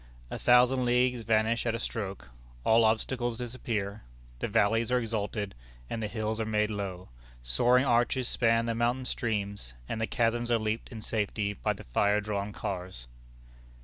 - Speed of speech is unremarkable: Yes, average, 165 wpm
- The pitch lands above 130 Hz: No, low, 110 Hz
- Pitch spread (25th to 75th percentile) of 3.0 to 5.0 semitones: No, narrow, 2.6 semitones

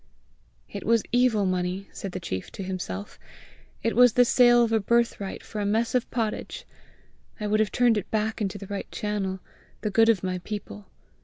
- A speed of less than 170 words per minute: No, average, 190 wpm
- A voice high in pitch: Yes, high, 210 Hz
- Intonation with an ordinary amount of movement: Yes, average, 3.2 semitones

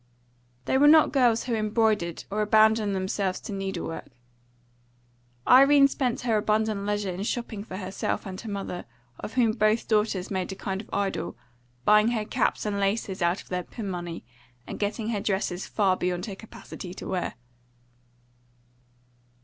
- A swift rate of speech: No, average, 165 wpm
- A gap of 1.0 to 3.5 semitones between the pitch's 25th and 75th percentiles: Yes, average, 2.7 semitones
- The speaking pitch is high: Yes, high, 205 Hz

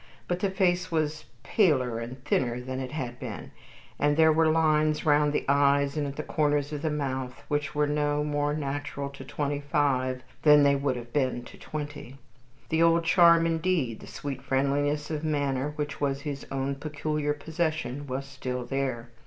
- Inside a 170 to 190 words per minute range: Yes, average, 180 wpm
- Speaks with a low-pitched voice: No, medium, 145 Hz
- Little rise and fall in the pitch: Yes, narrow, 2.2 semitones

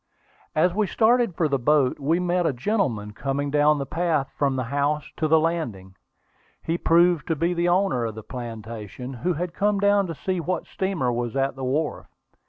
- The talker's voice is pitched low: No, medium, 150 Hz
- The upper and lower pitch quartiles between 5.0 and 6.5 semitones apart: Yes, average, 5.3 semitones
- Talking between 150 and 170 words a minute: No, average, 195 wpm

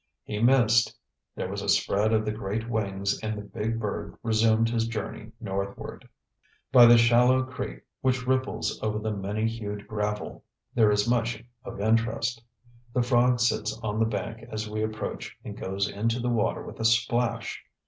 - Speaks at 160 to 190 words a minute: Yes, average, 170 wpm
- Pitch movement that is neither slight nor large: No, narrow, 2.0 semitones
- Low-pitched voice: Yes, low, 110 Hz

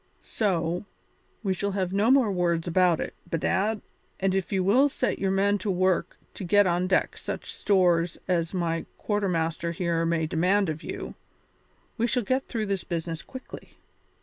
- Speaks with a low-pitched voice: No, medium, 185 Hz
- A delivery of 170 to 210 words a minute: Yes, average, 175 wpm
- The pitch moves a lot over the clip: No, average, 3.1 semitones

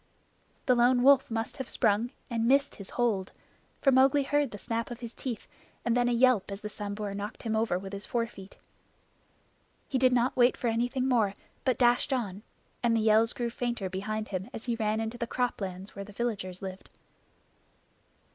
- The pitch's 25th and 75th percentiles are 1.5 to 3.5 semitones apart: Yes, average, 3.2 semitones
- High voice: Yes, high, 230 Hz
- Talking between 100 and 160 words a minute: No, average, 190 wpm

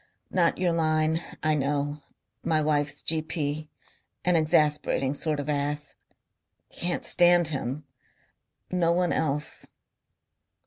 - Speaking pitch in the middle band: Yes, medium, 155 Hz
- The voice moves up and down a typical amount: No, narrow, 2.2 semitones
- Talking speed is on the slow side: Yes, slow, 105 wpm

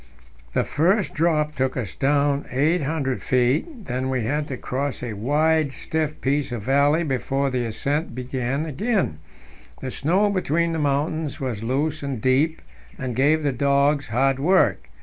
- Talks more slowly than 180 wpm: Yes, average, 155 wpm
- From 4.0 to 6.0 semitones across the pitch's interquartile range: No, average, 3.2 semitones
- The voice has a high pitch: No, medium, 140 Hz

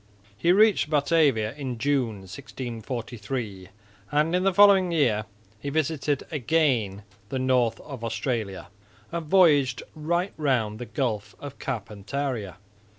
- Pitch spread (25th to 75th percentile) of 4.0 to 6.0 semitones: Yes, wide, 5.6 semitones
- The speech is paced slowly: Yes, slow, 120 wpm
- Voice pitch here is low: Yes, low, 130 Hz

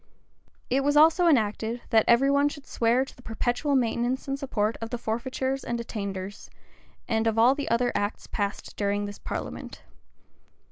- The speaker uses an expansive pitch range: No, average, 3.6 semitones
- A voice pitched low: No, high, 235 Hz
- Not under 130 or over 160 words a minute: No, average, 175 wpm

